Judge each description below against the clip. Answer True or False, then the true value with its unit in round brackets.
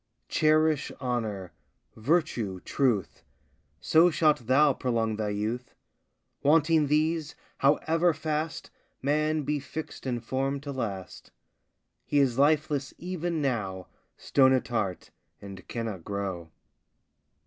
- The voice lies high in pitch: False (135 Hz)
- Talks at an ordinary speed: False (110 wpm)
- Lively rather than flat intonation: True (5.8 semitones)